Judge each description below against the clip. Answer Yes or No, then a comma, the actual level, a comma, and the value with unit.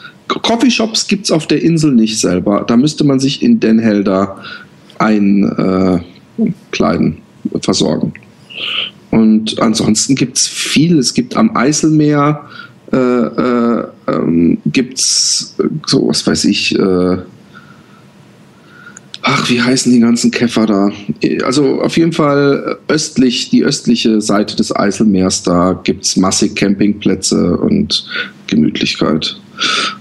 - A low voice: Yes, low, 110 Hz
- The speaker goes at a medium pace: No, slow, 120 wpm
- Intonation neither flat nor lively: No, wide, 6.1 semitones